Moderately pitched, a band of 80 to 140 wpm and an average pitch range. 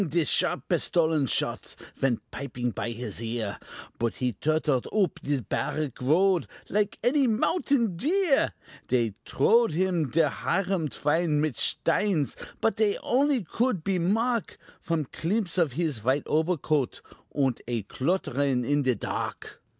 No: medium, 155 Hz; slow, 135 wpm; wide, 7.1 semitones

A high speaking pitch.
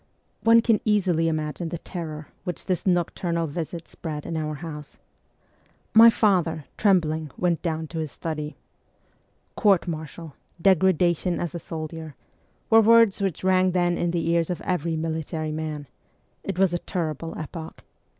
No: medium, 170 Hz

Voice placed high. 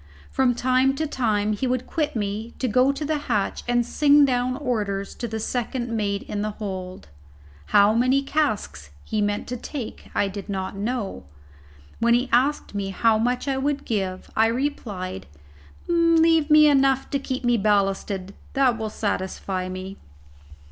Yes: high, 235 Hz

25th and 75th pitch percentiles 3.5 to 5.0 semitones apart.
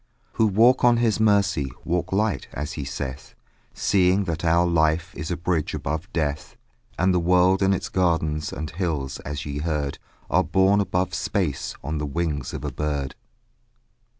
Yes: average, 3.9 semitones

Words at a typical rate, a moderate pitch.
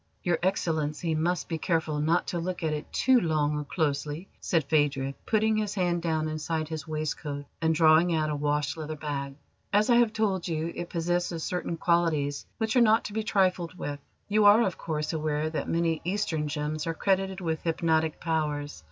Yes: average, 190 wpm; medium, 160 Hz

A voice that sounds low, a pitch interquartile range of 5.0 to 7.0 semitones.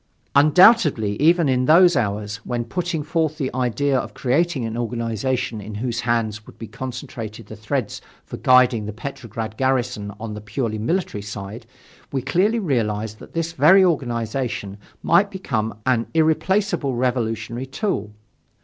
Yes: low, 125 Hz; wide, 5.5 semitones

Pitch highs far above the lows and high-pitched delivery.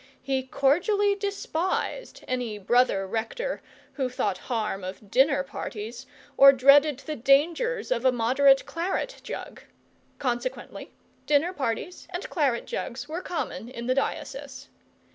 Yes: wide, 5.8 semitones; very high, 270 Hz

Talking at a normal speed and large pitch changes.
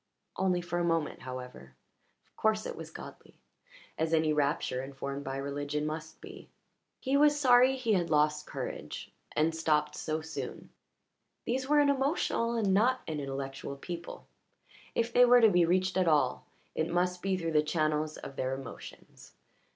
Yes: average, 165 wpm; wide, 6.3 semitones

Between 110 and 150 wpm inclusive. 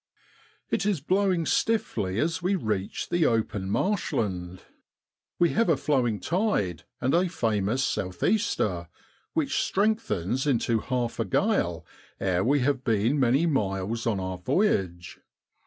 Yes: average, 140 wpm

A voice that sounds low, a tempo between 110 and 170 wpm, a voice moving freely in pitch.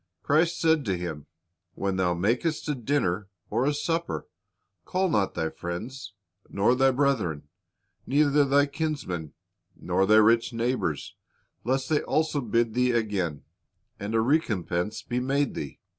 Yes: low, 120 Hz; average, 145 wpm; wide, 6.7 semitones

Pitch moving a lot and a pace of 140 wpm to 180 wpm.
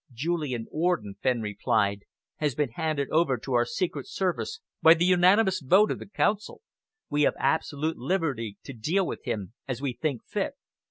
Yes: wide, 6.4 semitones; average, 170 wpm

